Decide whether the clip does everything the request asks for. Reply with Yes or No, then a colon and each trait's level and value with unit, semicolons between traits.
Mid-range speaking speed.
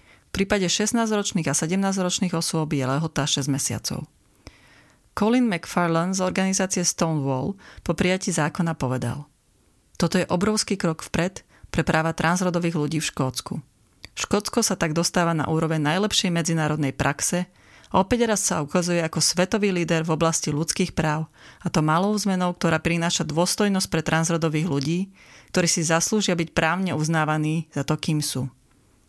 Yes: average, 145 wpm